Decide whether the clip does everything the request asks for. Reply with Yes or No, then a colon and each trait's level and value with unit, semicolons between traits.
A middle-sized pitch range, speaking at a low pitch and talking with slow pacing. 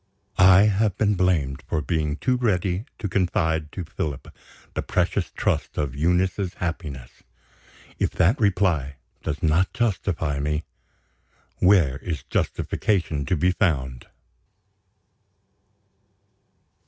Yes: average, 4.3 semitones; very low, 90 Hz; slow, 115 wpm